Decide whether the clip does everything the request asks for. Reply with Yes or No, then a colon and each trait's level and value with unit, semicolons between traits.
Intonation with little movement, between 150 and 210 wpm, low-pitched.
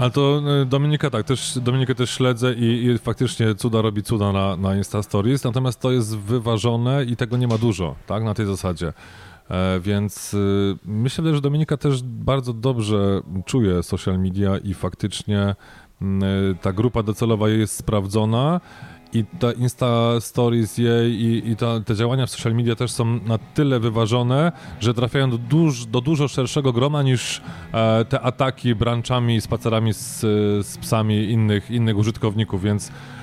No: average, 3.4 semitones; fast, 160 wpm; low, 115 Hz